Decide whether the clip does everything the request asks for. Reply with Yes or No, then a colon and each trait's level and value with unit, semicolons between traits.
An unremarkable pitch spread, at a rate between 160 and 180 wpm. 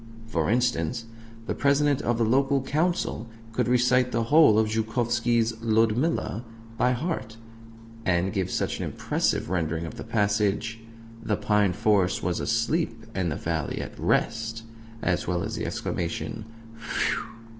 No: average, 3.5 semitones; average, 145 wpm